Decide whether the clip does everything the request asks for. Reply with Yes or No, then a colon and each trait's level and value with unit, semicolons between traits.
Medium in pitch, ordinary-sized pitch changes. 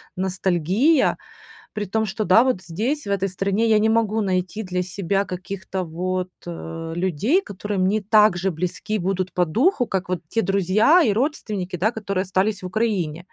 No: high, 195 Hz; average, 3.0 semitones